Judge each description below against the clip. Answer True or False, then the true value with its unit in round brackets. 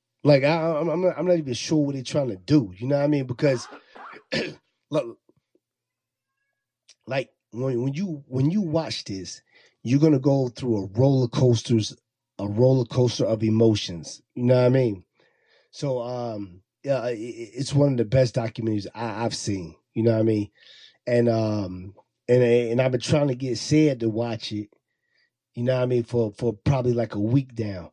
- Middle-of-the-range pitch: False (125 Hz)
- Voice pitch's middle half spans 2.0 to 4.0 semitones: True (3.6 semitones)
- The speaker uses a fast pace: False (190 wpm)